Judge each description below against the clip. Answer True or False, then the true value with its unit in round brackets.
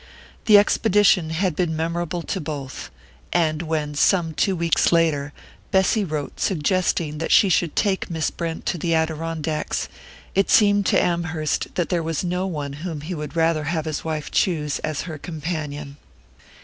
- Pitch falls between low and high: True (165 Hz)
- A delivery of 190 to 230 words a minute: False (160 wpm)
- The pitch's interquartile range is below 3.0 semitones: True (2.6 semitones)